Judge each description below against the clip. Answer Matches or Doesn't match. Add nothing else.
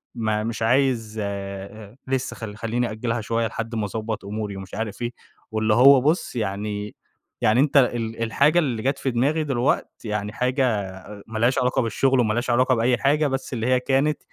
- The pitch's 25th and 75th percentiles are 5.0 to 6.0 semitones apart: Doesn't match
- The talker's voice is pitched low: Matches